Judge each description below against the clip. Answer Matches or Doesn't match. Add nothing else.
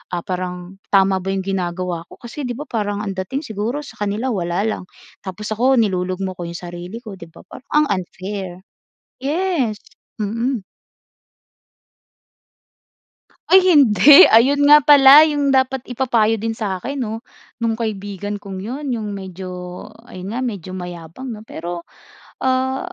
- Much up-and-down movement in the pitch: Matches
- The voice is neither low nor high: Doesn't match